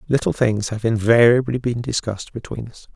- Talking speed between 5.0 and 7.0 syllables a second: Yes, 5.5 syllables/s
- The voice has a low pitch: Yes, low, 115 Hz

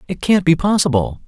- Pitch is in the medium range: Yes, medium, 165 Hz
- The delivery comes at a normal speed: Yes, average, 190 wpm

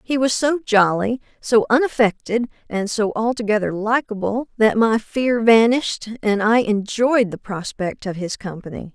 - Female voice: Yes, female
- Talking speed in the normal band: Yes, average, 150 wpm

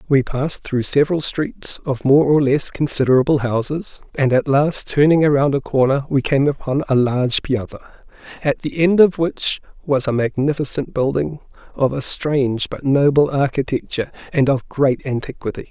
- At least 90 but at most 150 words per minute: No, average, 165 wpm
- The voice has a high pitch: No, medium, 140 Hz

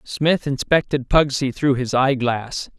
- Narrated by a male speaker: Yes, male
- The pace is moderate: No, slow, 130 wpm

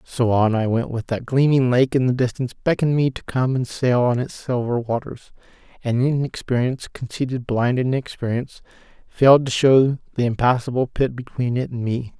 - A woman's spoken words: No, male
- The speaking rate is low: No, average, 175 wpm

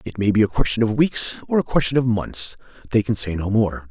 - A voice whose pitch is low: Yes, low, 115 Hz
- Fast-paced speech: Yes, fast, 260 wpm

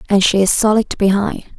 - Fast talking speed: No, average, 190 wpm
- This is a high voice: Yes, high, 200 Hz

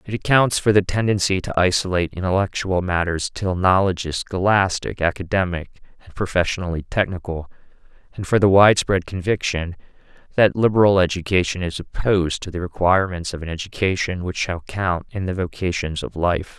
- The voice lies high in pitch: No, very low, 90 Hz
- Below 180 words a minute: Yes, average, 150 wpm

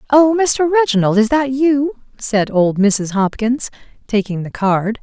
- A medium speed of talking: Yes, average, 155 wpm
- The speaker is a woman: Yes, female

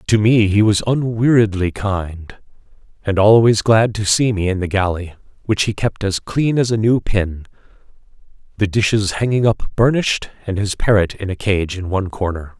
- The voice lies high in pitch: No, low, 105 Hz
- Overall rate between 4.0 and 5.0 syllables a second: Yes, 4.9 syllables/s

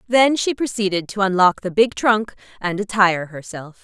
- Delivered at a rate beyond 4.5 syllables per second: Yes, 5.0 syllables/s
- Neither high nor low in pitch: No, high, 200 Hz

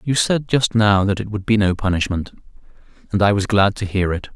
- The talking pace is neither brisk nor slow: No, fast, 235 wpm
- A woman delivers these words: No, male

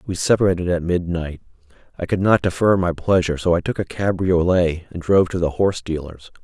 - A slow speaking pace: No, average, 195 wpm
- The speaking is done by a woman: No, male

